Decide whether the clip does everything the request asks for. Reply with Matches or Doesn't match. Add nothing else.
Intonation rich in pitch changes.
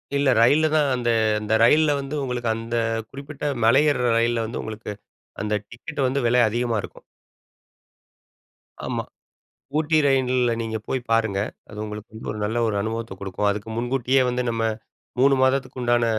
Doesn't match